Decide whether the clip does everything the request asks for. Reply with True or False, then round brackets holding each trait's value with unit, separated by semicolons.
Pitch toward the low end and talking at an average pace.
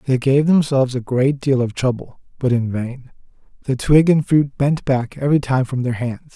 False (130 Hz; 210 wpm)